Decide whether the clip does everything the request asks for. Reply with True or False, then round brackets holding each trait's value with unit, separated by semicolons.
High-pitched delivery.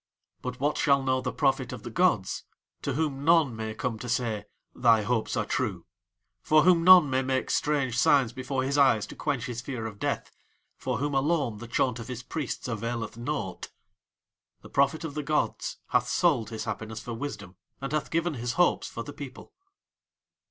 False (130 Hz)